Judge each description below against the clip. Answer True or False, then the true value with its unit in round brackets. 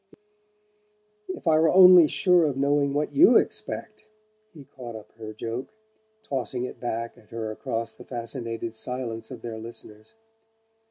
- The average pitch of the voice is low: True (120 Hz)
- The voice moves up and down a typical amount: True (4.2 semitones)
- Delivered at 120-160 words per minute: True (150 wpm)